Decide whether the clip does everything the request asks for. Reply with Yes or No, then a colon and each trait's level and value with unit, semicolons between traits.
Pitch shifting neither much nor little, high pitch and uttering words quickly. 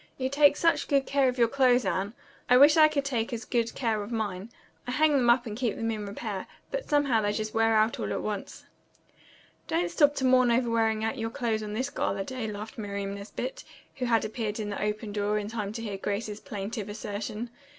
Yes: average, 3.6 semitones; high, 225 Hz; fast, 225 wpm